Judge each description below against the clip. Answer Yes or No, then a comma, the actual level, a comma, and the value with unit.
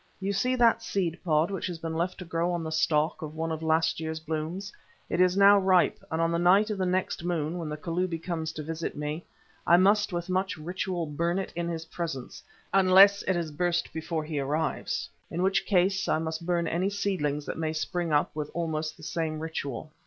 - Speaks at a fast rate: Yes, fast, 220 wpm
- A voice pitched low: No, medium, 170 Hz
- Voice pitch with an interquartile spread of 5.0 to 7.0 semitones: No, average, 2.7 semitones